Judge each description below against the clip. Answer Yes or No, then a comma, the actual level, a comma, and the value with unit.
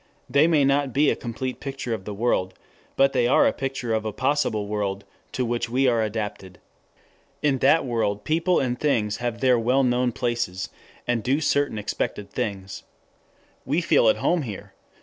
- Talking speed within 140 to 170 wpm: No, average, 180 wpm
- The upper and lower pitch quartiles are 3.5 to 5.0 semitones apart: Yes, average, 4.2 semitones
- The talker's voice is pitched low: Yes, low, 120 Hz